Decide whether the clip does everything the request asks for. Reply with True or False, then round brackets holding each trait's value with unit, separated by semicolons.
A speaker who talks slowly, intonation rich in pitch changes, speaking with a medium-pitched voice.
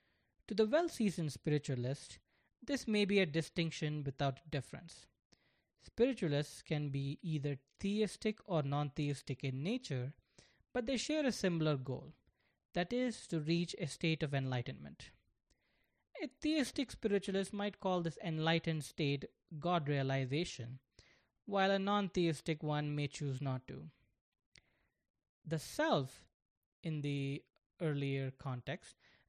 True (125 wpm; 6.0 semitones; 160 Hz)